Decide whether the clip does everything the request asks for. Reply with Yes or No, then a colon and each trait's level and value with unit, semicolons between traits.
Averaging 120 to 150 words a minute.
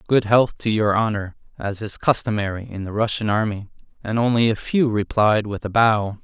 No: average, 190 wpm